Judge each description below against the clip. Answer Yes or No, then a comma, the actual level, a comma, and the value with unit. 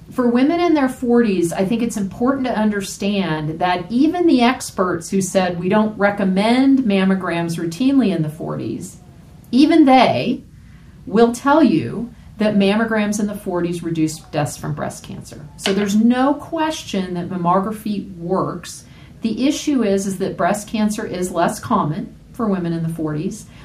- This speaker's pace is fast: No, average, 155 wpm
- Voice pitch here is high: Yes, high, 205 Hz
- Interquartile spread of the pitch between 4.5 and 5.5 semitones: Yes, average, 5.0 semitones